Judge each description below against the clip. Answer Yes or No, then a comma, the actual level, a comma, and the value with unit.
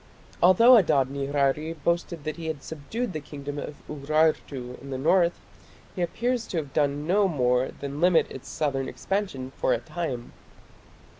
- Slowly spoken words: No, average, 160 wpm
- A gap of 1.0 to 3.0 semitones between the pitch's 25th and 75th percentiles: No, average, 3.9 semitones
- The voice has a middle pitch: Yes, medium, 150 Hz